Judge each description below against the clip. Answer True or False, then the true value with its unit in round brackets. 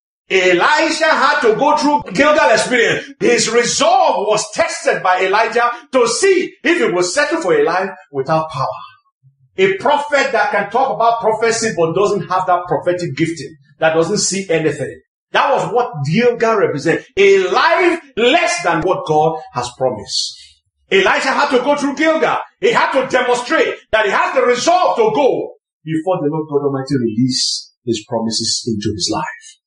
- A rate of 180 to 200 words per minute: False (165 wpm)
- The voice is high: True (220 Hz)